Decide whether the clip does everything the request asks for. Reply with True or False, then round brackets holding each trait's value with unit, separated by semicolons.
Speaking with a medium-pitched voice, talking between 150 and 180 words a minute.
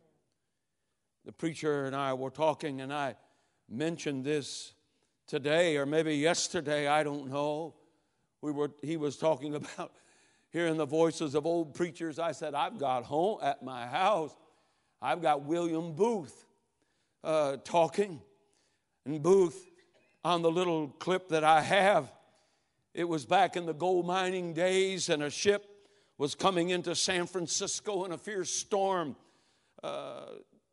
False (165 Hz; 140 wpm)